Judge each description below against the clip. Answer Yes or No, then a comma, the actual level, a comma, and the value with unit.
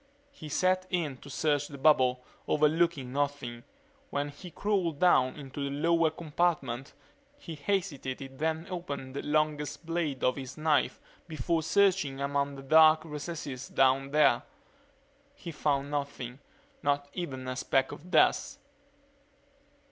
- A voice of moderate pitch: Yes, medium, 145 Hz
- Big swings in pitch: No, average, 3.2 semitones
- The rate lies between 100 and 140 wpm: Yes, slow, 135 wpm